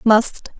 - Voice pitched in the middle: No, high, 225 Hz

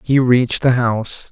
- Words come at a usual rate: Yes, average, 185 wpm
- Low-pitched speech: Yes, low, 125 Hz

